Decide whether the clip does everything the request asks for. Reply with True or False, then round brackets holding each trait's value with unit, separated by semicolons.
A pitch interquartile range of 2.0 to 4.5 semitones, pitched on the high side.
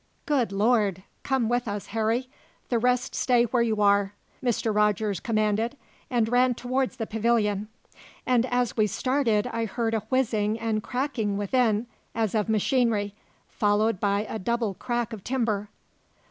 True (2.8 semitones; 225 Hz)